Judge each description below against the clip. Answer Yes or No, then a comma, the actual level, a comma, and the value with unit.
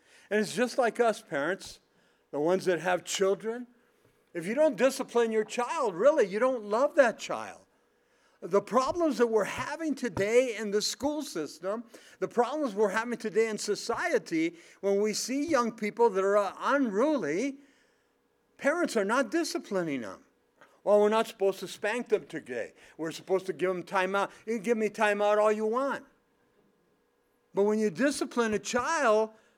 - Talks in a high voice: Yes, high, 220 Hz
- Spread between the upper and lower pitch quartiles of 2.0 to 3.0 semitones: No, average, 4.3 semitones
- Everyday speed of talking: Yes, average, 170 wpm